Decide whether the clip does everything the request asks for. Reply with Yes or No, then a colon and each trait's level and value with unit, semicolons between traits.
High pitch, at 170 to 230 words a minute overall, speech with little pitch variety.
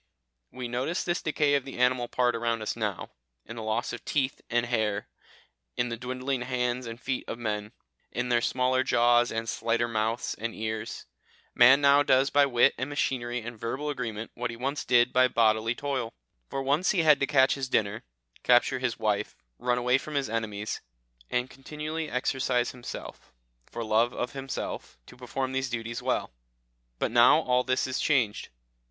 No: low, 125 Hz; average, 180 wpm; narrow, 2.3 semitones